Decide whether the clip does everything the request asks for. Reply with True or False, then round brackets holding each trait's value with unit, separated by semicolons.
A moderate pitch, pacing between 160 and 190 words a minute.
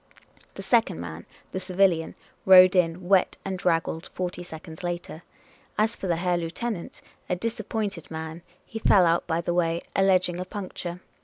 True (180 Hz; 165 wpm)